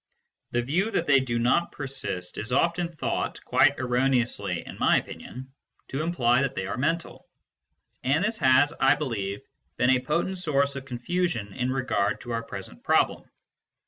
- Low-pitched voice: Yes, low, 130 Hz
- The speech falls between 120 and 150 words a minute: No, average, 165 wpm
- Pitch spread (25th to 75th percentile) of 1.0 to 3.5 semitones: No, average, 4.0 semitones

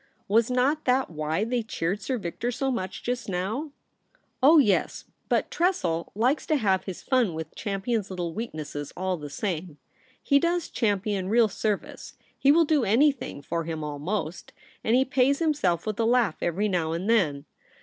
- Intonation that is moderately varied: No, wide, 6.5 semitones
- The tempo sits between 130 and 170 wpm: No, average, 180 wpm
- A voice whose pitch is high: Yes, high, 210 Hz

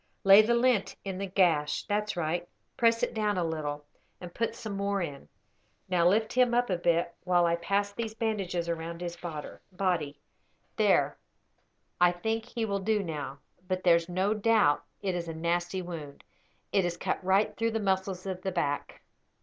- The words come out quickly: No, average, 180 wpm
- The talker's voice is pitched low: No, medium, 185 Hz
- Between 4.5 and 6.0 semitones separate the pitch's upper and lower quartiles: No, average, 3.4 semitones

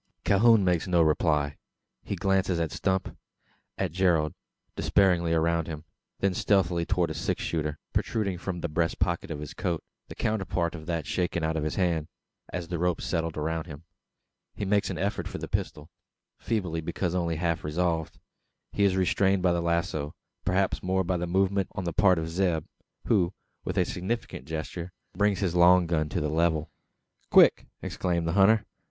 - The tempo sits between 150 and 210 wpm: Yes, average, 180 wpm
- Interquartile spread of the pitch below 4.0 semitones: Yes, narrow, 2.6 semitones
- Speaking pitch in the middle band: No, very low, 85 Hz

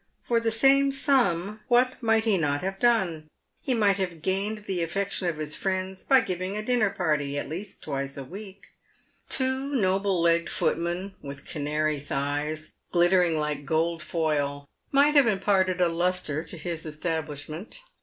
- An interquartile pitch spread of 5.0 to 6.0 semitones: Yes, average, 5.3 semitones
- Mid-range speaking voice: Yes, medium, 180 Hz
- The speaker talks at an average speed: Yes, average, 165 wpm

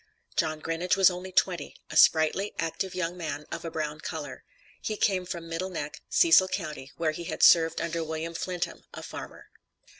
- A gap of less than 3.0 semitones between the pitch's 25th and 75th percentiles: Yes, narrow, 2.5 semitones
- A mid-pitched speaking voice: Yes, medium, 165 Hz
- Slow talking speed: No, average, 180 wpm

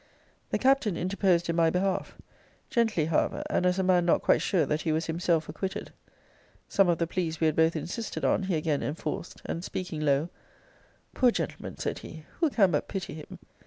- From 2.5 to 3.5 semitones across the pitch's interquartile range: Yes, average, 3.1 semitones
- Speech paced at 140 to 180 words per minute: No, average, 195 wpm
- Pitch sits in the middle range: Yes, medium, 170 Hz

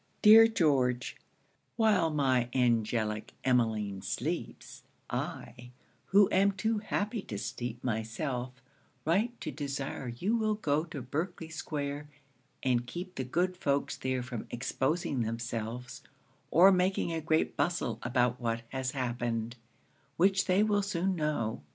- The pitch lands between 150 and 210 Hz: No, medium, 140 Hz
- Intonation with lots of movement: Yes, wide, 7.0 semitones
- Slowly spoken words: Yes, slow, 130 wpm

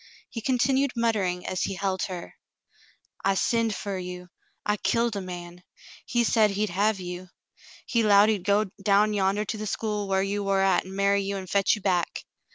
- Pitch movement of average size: No, narrow, 2.2 semitones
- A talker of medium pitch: No, high, 200 Hz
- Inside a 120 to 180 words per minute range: No, average, 190 wpm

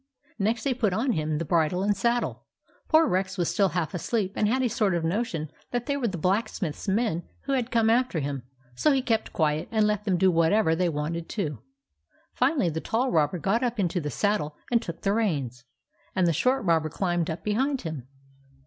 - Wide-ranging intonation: Yes, wide, 5.9 semitones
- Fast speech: Yes, fast, 210 wpm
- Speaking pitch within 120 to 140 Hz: No, high, 190 Hz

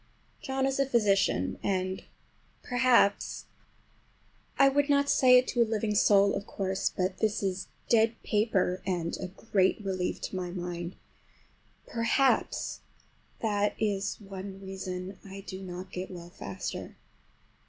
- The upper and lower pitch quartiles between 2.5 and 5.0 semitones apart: Yes, average, 3.5 semitones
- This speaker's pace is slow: Yes, slow, 130 wpm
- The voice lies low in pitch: No, high, 195 Hz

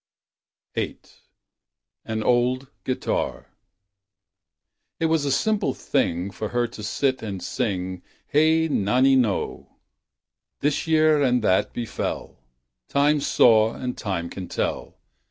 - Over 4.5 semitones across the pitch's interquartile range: Yes, wide, 5.5 semitones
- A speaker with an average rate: No, slow, 120 wpm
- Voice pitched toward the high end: No, low, 125 Hz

